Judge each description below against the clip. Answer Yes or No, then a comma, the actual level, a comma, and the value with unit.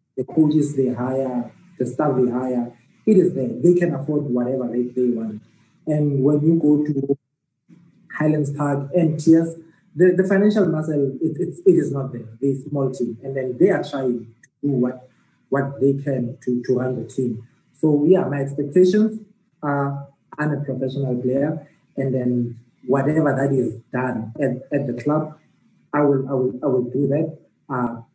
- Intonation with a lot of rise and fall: No, average, 3.3 semitones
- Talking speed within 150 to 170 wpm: No, average, 180 wpm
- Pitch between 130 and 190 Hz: Yes, medium, 140 Hz